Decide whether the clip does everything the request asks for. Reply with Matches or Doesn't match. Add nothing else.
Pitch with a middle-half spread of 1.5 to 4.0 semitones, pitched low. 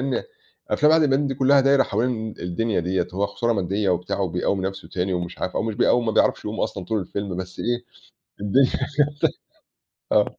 Doesn't match